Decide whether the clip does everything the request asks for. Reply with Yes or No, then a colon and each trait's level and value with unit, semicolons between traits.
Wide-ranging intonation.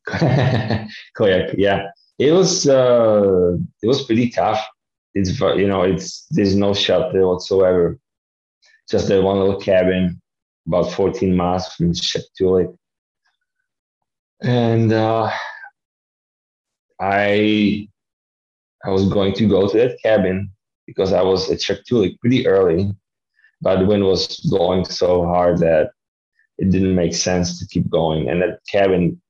No: average, 3.2 semitones